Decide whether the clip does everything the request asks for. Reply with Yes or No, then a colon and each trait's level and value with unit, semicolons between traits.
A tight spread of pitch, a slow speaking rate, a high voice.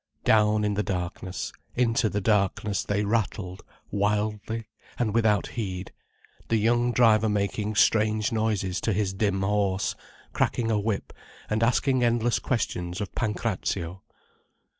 No: narrow, 2.2 semitones; slow, 130 wpm; low, 105 Hz